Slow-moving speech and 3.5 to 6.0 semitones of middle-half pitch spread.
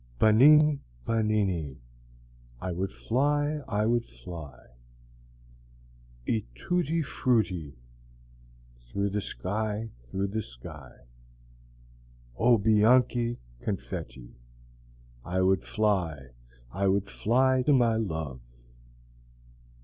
Yes: slow, 90 wpm; wide, 5.5 semitones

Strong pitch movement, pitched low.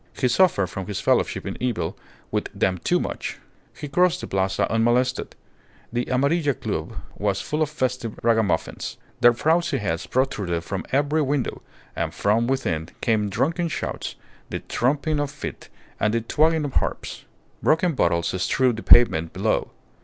Yes: wide, 6.2 semitones; low, 125 Hz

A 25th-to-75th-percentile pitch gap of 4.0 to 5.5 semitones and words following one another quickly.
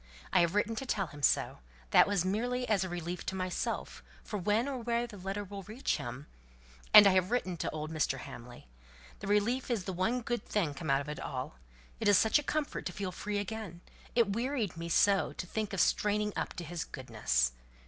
Yes: average, 4.4 semitones; fast, 220 wpm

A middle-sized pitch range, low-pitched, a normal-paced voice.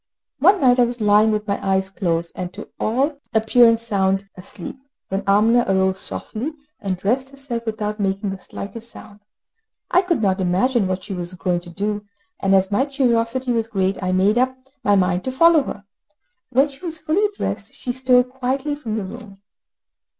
No: average, 4.9 semitones; high, 215 Hz; average, 185 wpm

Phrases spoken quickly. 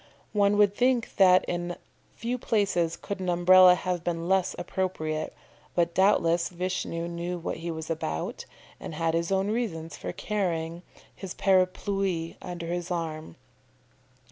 No: average, 145 wpm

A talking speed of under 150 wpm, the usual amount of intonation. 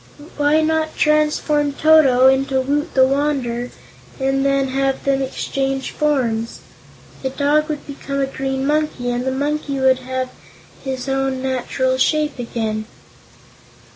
No: slow, 135 wpm; narrow, 2.1 semitones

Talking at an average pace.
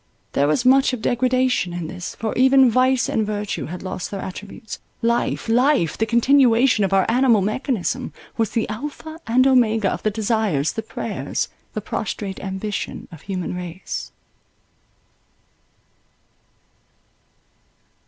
No: slow, 125 wpm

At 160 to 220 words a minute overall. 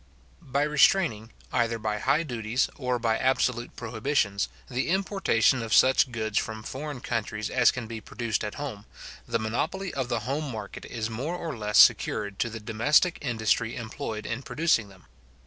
Yes: average, 165 wpm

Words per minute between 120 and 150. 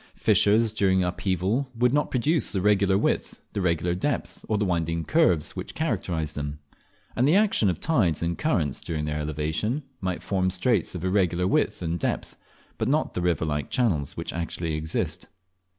No: average, 175 wpm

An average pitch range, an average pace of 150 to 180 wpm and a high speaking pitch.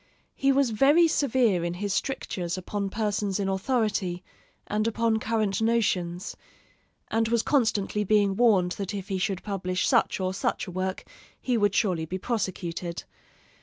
Yes: average, 3.4 semitones; average, 155 wpm; high, 205 Hz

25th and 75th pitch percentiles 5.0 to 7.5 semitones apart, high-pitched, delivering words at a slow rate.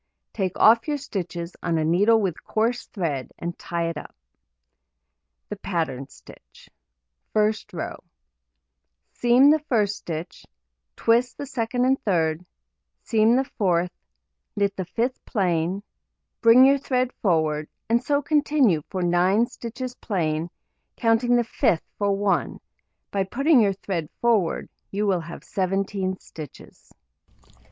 Yes: wide, 5.6 semitones; high, 200 Hz; slow, 130 wpm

